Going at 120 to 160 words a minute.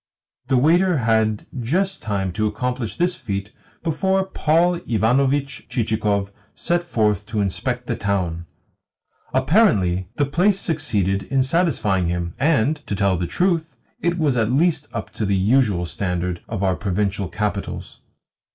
Yes: average, 140 wpm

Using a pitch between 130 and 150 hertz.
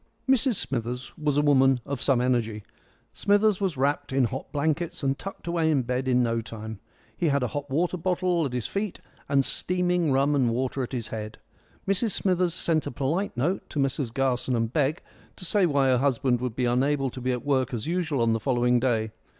Yes: low, 135 Hz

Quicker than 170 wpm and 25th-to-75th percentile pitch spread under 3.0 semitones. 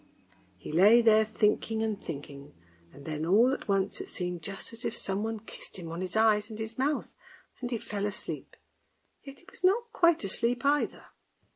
No: average, 185 wpm; average, 4.0 semitones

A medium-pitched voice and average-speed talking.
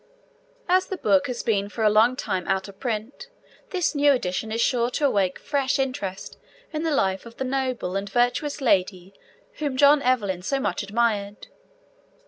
No: high, 235 Hz; average, 175 wpm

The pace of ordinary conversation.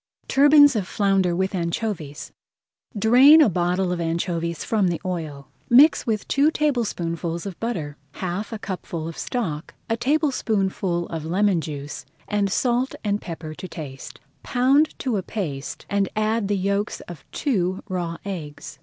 Yes: average, 150 wpm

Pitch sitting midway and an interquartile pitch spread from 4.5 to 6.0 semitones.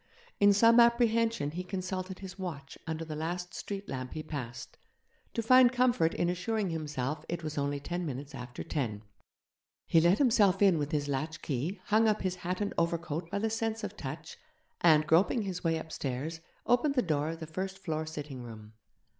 Yes: medium, 170 Hz; average, 5.1 semitones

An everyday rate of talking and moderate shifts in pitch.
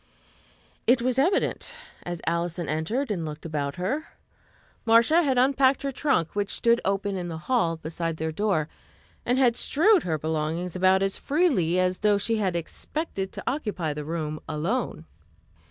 No: average, 160 wpm; wide, 7.5 semitones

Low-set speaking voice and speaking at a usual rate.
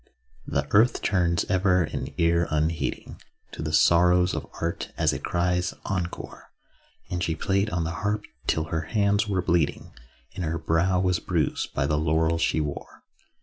Yes: very low, 85 Hz; average, 165 wpm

